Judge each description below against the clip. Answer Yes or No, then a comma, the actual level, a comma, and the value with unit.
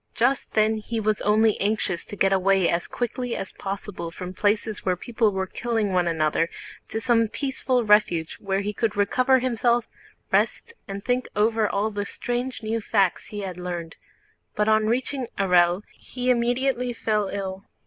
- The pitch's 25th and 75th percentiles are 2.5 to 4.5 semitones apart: Yes, average, 3.6 semitones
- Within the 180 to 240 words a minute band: No, average, 170 wpm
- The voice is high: Yes, high, 210 Hz